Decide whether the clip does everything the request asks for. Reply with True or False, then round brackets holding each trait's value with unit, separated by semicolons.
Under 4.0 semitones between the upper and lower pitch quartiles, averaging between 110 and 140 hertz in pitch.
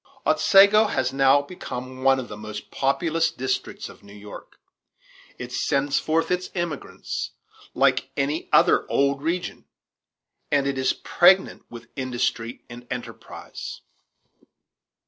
False (4.6 semitones; 135 Hz)